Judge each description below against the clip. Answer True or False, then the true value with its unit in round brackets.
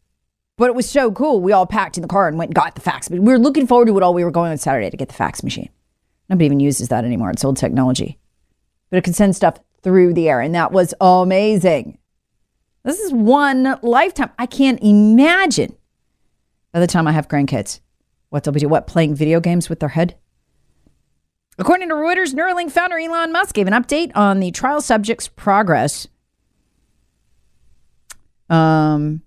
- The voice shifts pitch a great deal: True (8.1 semitones)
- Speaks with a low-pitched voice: False (185 Hz)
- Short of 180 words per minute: False (195 wpm)